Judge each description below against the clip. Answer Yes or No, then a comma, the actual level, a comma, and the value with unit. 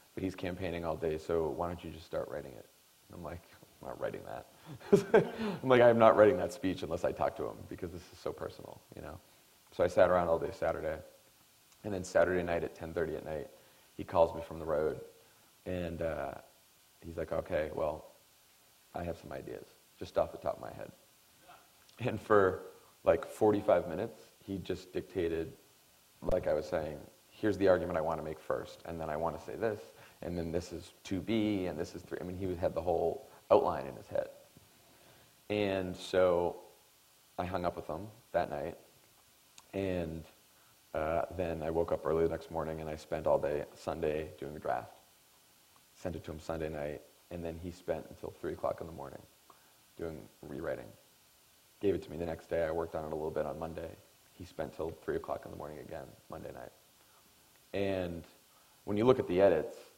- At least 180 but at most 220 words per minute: Yes, average, 200 wpm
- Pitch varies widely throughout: No, average, 3.2 semitones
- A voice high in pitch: No, very low, 90 Hz